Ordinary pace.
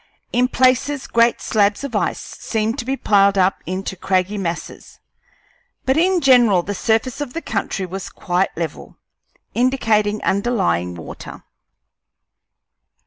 No: slow, 130 wpm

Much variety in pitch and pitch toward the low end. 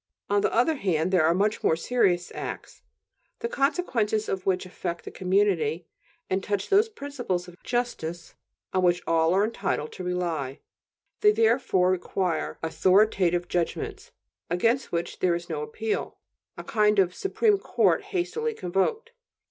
No: wide, 5.7 semitones; high, 190 Hz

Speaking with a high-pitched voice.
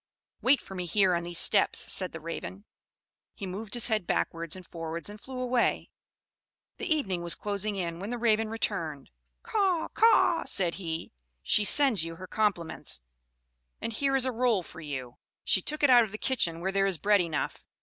Yes: high, 195 Hz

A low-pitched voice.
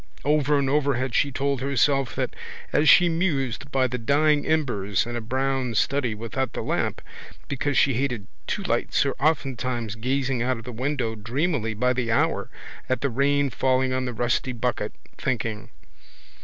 Yes: low, 130 Hz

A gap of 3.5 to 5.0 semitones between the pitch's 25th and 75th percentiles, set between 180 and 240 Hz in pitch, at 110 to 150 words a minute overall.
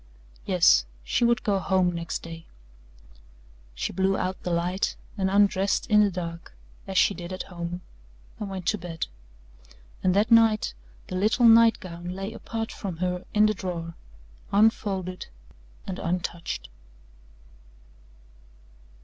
No: average, 2.9 semitones; high, 190 Hz; slow, 135 wpm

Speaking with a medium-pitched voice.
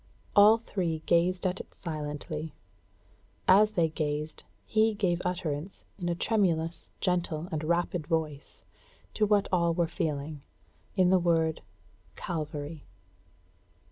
Yes: medium, 170 Hz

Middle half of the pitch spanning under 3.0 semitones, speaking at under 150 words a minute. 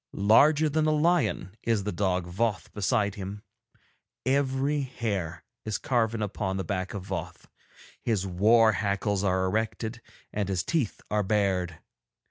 No: average, 3.8 semitones; average, 140 wpm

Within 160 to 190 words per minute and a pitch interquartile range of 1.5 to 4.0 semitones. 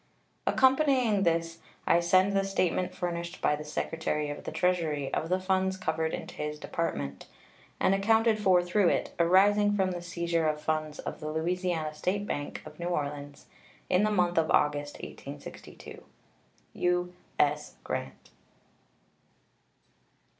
No: average, 140 wpm; average, 3.6 semitones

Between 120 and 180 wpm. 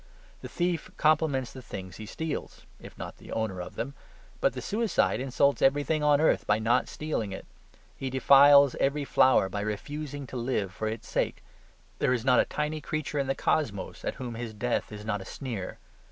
No: average, 195 wpm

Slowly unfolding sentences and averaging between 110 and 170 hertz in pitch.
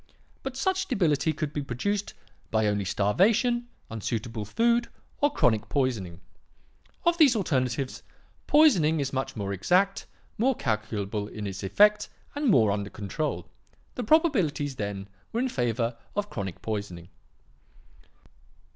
Yes: slow, 130 wpm; low, 135 Hz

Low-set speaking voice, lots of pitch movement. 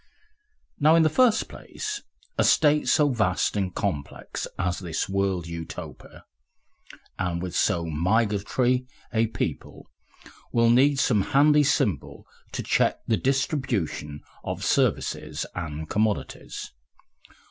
Yes: low, 105 Hz; wide, 7.7 semitones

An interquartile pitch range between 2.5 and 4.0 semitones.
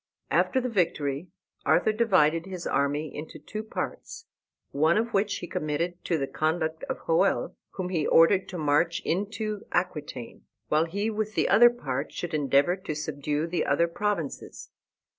No: average, 4.9 semitones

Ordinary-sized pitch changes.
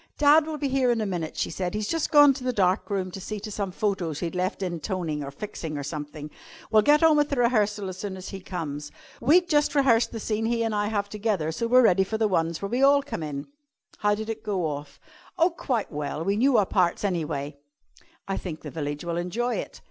No: wide, 5.9 semitones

